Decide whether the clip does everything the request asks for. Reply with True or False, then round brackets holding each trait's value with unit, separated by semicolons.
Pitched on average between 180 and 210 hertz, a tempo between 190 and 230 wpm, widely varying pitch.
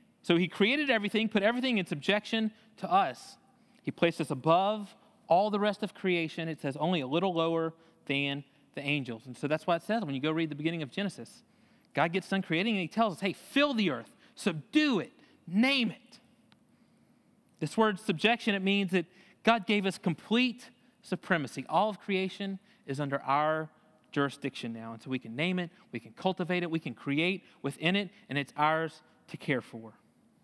True (185 Hz; 195 wpm; 5.8 semitones)